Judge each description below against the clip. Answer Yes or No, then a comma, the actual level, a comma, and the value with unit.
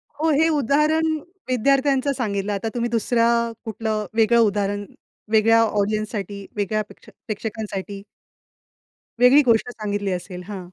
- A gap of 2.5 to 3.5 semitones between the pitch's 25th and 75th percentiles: Yes, average, 3.0 semitones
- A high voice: Yes, high, 220 Hz